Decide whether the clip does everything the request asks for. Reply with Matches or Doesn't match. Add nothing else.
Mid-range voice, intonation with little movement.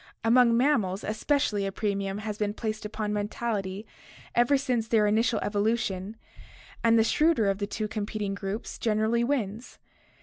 Doesn't match